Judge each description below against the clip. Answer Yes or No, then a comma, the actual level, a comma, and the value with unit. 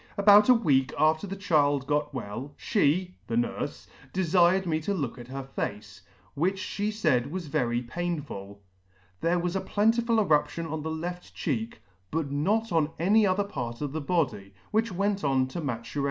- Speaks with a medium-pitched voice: Yes, medium, 160 Hz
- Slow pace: No, average, 175 wpm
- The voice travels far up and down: Yes, wide, 6.1 semitones